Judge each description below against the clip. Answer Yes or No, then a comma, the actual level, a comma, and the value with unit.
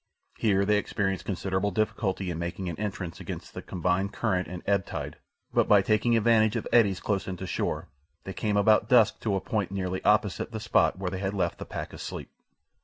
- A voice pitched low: Yes, low, 100 Hz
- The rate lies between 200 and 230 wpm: Yes, fast, 205 wpm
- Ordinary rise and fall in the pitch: No, narrow, 2.3 semitones